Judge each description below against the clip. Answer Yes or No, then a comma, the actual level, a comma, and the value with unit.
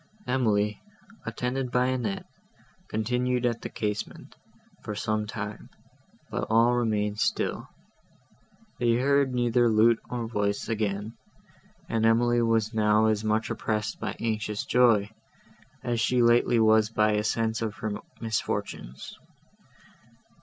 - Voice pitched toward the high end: No, low, 110 Hz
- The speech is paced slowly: Yes, slow, 125 wpm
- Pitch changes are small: Yes, narrow, 2.1 semitones